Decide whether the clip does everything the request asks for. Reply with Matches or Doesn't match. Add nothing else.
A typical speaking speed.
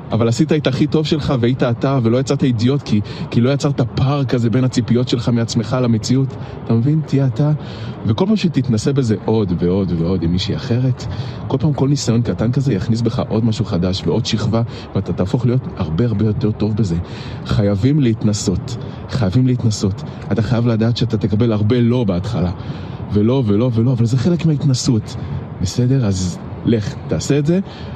Doesn't match